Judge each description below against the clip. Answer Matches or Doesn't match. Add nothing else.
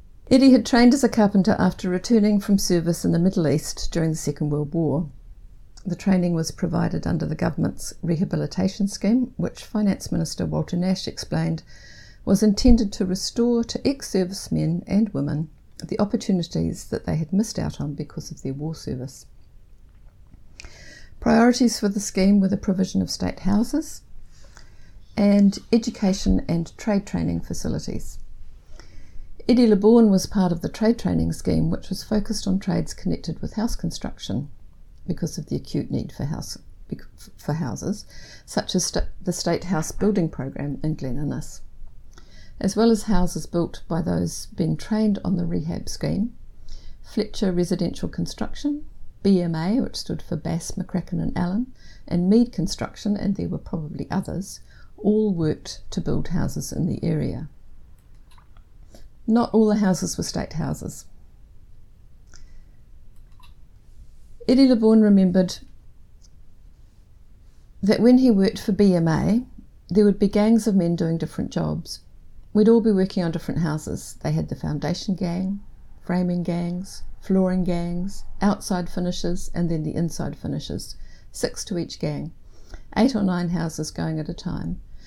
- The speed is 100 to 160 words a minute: Matches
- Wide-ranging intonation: Matches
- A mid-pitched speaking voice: Matches